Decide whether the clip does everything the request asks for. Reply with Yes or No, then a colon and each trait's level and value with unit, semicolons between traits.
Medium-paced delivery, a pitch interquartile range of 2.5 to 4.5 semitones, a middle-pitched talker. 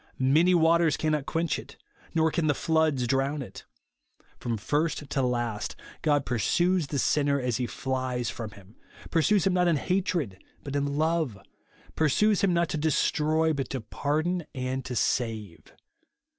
Yes: average, 160 wpm; average, 4.1 semitones; medium, 145 Hz